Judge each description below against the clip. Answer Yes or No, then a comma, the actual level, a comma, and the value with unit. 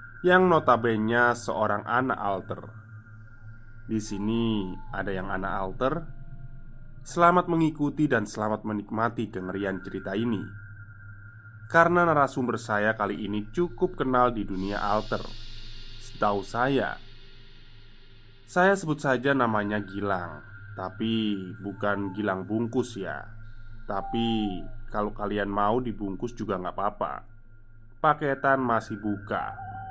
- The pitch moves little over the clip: No, average, 3.1 semitones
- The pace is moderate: Yes, average, 105 wpm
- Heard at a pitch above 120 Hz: No, low, 110 Hz